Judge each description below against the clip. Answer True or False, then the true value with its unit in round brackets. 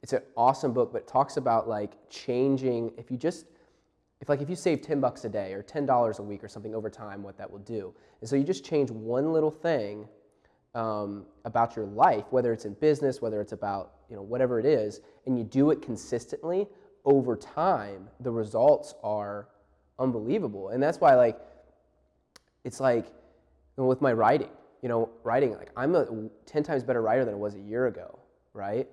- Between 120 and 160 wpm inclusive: False (195 wpm)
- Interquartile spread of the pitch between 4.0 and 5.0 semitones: True (4.7 semitones)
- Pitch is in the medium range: False (115 Hz)